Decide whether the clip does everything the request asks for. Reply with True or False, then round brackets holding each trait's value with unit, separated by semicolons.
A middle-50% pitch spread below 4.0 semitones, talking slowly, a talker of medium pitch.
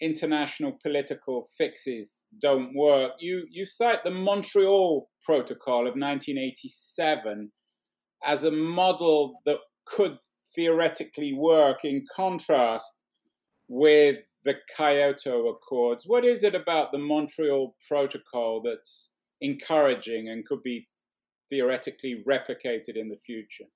False (5.4 semitones; 110 wpm; 150 Hz)